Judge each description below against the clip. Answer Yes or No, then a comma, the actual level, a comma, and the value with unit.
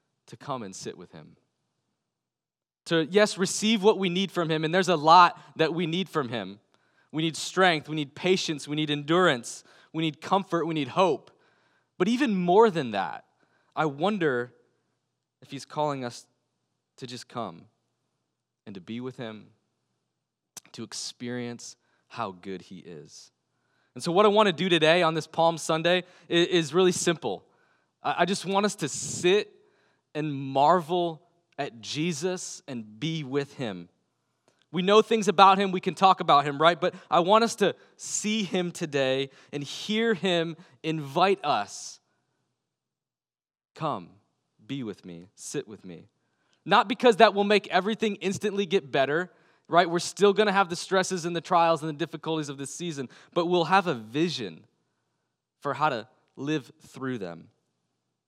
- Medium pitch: Yes, medium, 170 Hz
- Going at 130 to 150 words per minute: No, average, 165 wpm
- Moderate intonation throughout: Yes, average, 5.0 semitones